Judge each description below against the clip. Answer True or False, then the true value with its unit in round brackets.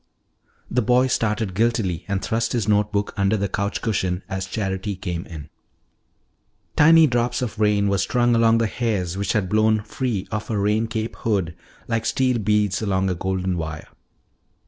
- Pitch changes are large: False (3.2 semitones)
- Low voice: True (105 Hz)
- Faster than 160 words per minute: True (170 wpm)